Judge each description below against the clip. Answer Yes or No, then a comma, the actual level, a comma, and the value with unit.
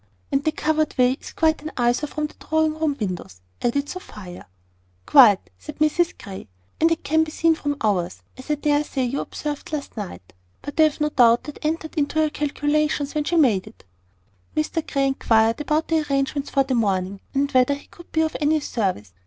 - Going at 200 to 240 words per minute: Yes, fast, 205 wpm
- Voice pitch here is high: Yes, very high, 290 Hz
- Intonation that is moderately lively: Yes, average, 4.3 semitones